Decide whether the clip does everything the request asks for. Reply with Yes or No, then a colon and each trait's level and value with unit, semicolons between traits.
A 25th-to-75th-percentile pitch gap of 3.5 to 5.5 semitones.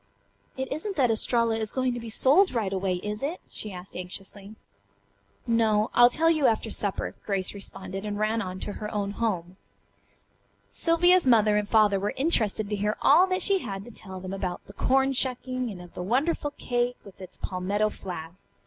Yes: average, 4.6 semitones